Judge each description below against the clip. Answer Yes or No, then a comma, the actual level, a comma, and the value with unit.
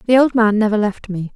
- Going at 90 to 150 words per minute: No, fast, 265 wpm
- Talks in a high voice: Yes, high, 215 Hz